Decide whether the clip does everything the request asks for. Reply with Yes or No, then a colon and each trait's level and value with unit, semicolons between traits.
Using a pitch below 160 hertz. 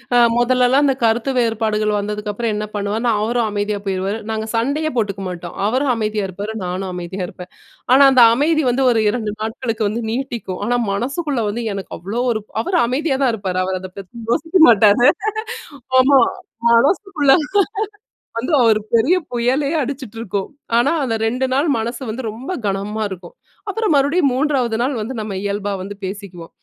No: high, 225 Hz